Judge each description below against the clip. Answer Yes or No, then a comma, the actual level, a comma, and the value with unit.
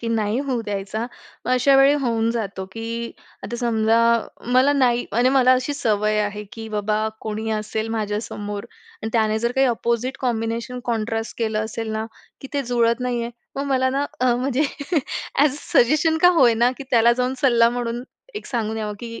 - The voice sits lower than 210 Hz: No, high, 235 Hz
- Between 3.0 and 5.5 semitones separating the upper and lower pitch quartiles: No, narrow, 2.6 semitones